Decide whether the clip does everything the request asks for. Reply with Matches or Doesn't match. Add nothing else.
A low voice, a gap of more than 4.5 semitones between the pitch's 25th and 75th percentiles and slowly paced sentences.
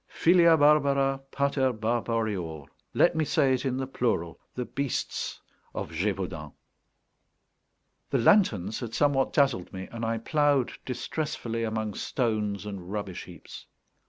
Matches